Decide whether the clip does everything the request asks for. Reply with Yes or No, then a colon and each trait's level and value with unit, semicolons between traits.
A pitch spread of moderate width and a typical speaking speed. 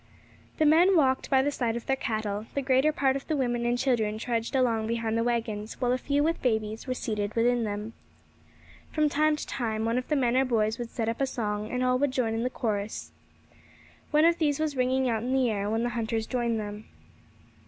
No: average, 3.2 semitones; fast, 225 wpm